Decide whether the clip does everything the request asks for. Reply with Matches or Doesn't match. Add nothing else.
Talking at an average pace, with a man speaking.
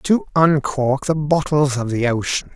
Matches